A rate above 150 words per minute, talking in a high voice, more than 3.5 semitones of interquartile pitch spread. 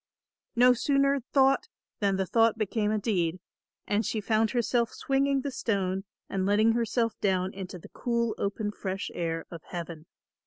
Yes: average, 160 wpm; high, 215 Hz; average, 3.9 semitones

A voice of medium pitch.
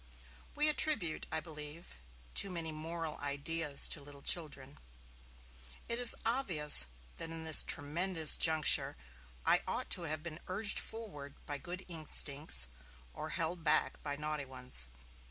Yes: medium, 160 Hz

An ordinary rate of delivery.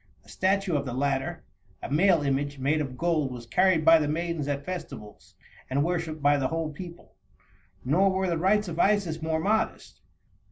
Yes: average, 185 wpm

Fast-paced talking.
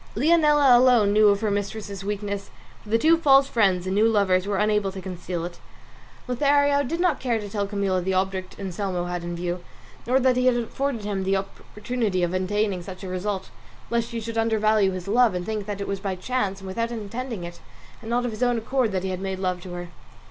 Yes: fast, 225 wpm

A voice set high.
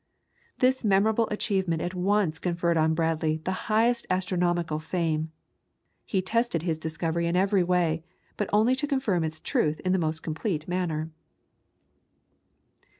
No: medium, 180 Hz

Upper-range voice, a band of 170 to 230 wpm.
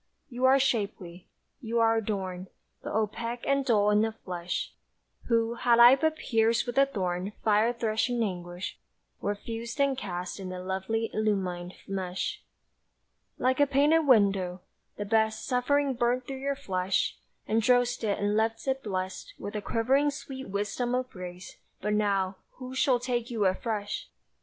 No: high, 225 Hz; average, 155 wpm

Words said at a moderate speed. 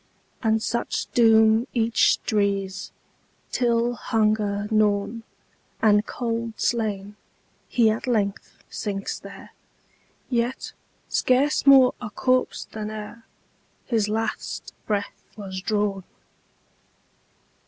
No: slow, 80 wpm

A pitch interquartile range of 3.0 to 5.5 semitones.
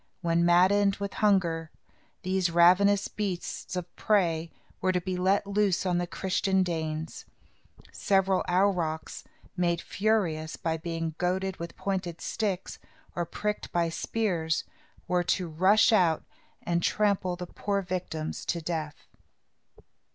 No: narrow, 2.6 semitones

